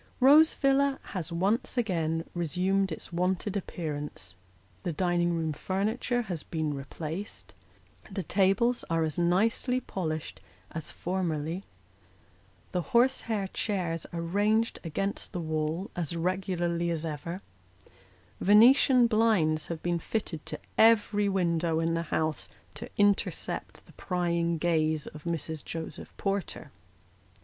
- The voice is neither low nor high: Yes, medium, 175 Hz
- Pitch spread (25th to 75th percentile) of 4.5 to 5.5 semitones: No, average, 3.9 semitones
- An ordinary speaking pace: No, slow, 120 wpm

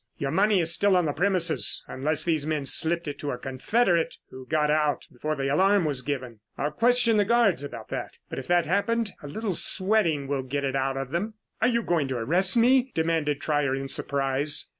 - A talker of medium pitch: Yes, medium, 155 Hz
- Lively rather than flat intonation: Yes, wide, 5.9 semitones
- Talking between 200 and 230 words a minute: Yes, fast, 205 wpm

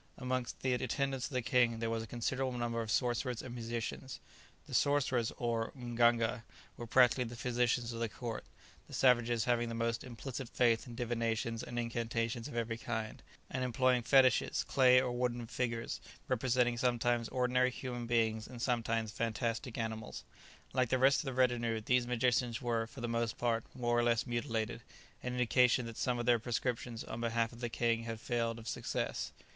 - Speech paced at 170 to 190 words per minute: Yes, average, 180 wpm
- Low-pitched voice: Yes, low, 120 Hz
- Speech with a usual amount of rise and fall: No, narrow, 1.4 semitones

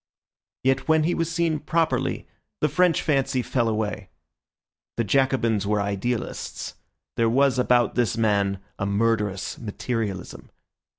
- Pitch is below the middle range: Yes, low, 120 Hz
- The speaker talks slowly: Yes, slow, 125 wpm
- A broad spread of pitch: No, average, 4.9 semitones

